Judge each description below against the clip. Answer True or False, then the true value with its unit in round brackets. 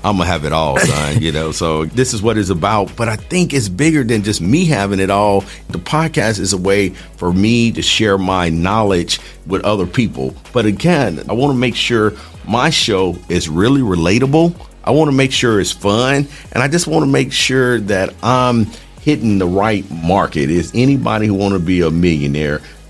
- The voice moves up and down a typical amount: False (5.9 semitones)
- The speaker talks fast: False (195 wpm)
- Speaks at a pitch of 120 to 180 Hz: False (105 Hz)